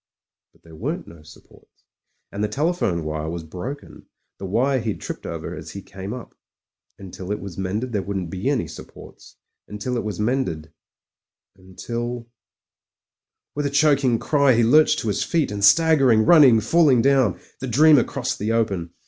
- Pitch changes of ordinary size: No, wide, 5.9 semitones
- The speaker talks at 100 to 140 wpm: No, average, 175 wpm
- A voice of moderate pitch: No, low, 115 Hz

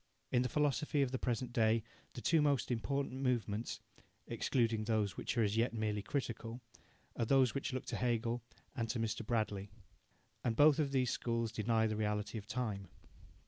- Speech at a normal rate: Yes, average, 180 wpm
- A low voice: Yes, low, 115 Hz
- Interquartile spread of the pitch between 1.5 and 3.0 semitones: Yes, average, 2.7 semitones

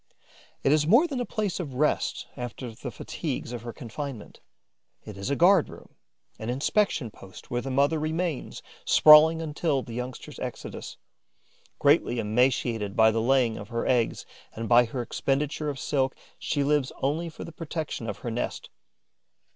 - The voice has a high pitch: No, low, 135 Hz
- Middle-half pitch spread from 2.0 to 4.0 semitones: No, average, 4.6 semitones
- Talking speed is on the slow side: No, average, 165 wpm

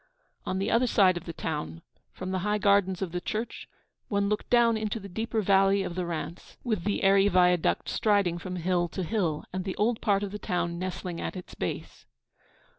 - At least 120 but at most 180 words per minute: No, fast, 205 wpm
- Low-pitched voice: No, high, 190 Hz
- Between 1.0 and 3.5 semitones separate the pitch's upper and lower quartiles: Yes, average, 2.7 semitones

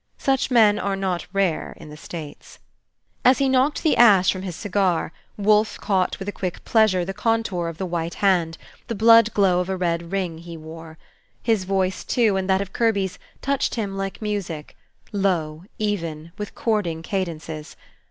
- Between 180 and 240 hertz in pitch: Yes, high, 190 Hz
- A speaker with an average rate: Yes, average, 175 wpm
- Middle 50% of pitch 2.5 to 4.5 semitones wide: Yes, average, 3.7 semitones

